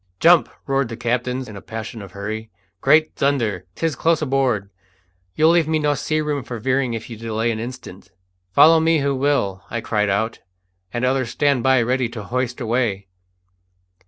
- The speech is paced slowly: No, average, 180 wpm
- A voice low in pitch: Yes, low, 125 Hz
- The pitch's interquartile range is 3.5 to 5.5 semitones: Yes, average, 4.2 semitones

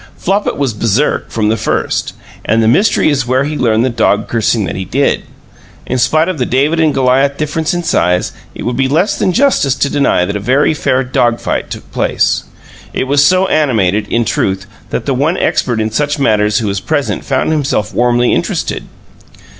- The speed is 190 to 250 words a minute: Yes, average, 200 wpm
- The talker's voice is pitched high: No, low, 130 Hz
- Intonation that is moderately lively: Yes, average, 5.0 semitones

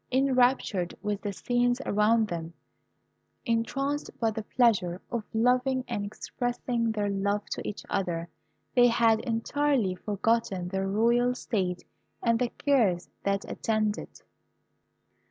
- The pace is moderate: No, slow, 125 wpm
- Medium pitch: No, high, 225 Hz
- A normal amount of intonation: Yes, average, 3.5 semitones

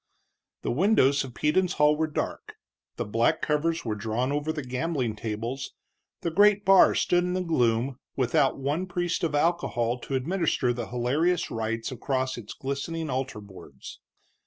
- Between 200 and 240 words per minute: No, average, 160 wpm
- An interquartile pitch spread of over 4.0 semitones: Yes, wide, 5.4 semitones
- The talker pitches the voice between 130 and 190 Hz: Yes, medium, 140 Hz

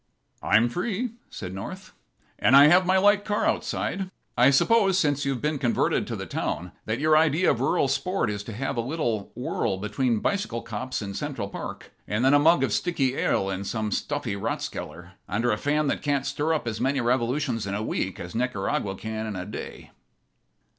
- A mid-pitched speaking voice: No, low, 130 Hz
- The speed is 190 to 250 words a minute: Yes, average, 195 wpm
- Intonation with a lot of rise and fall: Yes, wide, 6.0 semitones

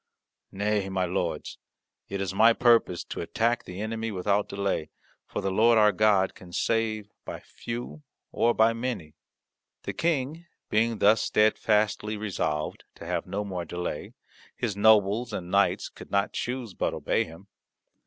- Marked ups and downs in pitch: No, average, 2.8 semitones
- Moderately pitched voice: No, low, 105 Hz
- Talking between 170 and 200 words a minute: No, average, 155 wpm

